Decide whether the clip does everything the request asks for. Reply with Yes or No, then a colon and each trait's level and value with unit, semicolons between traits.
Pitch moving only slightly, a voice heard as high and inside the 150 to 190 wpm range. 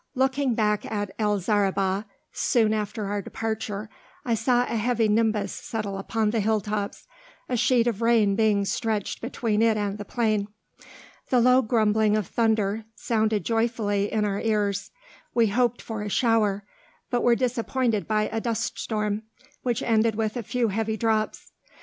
Yes: narrow, 1.9 semitones; high, 220 Hz; average, 160 wpm